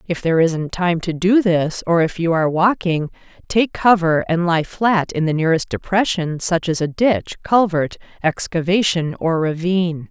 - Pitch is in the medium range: Yes, medium, 175 Hz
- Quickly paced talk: No, average, 160 wpm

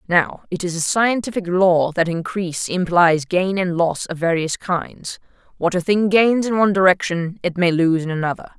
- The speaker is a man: No, female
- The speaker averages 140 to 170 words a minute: No, average, 190 wpm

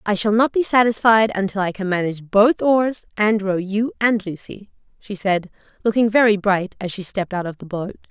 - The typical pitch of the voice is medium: No, high, 205 Hz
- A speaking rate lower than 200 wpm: No, fast, 205 wpm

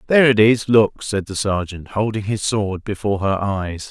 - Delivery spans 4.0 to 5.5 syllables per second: Yes, 4.9 syllables/s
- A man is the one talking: Yes, male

